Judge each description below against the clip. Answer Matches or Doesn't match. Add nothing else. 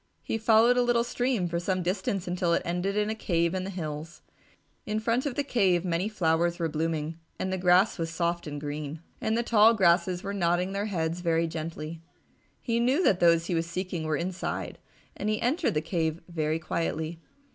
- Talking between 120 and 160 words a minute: Doesn't match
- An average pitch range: Matches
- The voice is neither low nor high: Matches